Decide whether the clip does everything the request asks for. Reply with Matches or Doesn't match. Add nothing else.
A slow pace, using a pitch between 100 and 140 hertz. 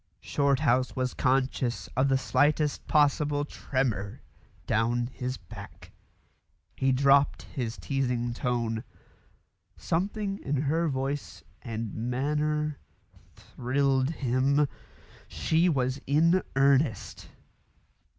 Matches